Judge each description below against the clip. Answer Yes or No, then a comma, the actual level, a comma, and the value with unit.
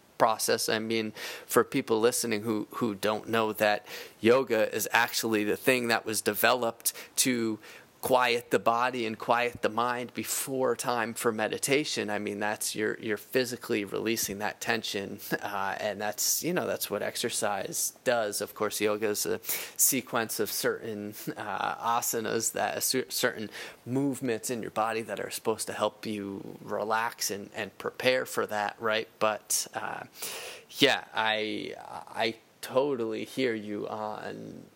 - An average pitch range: No, narrow, 2.1 semitones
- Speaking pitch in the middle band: No, low, 110 Hz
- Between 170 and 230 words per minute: No, average, 150 wpm